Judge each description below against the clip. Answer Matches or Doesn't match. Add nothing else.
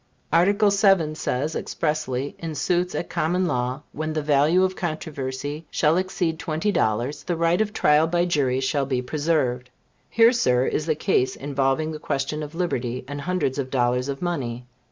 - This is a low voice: Doesn't match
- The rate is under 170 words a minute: Doesn't match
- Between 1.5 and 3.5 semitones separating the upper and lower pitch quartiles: Doesn't match